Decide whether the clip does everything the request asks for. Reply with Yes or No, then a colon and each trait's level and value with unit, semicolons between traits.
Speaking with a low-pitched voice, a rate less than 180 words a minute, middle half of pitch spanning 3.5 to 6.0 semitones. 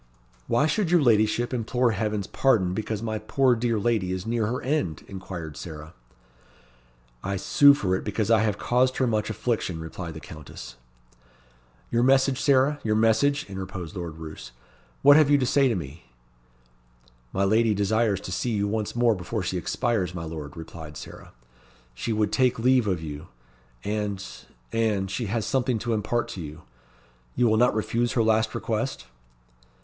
Yes: low, 110 Hz; average, 170 wpm; average, 4.6 semitones